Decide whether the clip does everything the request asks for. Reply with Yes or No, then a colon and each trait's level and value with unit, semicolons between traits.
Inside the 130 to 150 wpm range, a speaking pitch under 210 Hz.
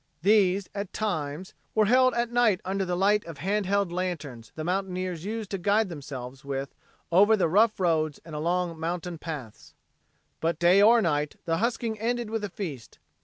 No: average, 170 wpm; medium, 185 Hz